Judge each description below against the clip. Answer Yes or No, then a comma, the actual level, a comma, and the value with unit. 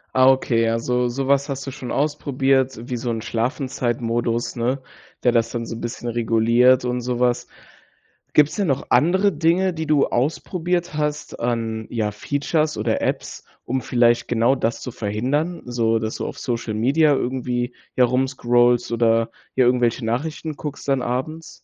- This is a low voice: Yes, low, 125 Hz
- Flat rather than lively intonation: No, average, 3.3 semitones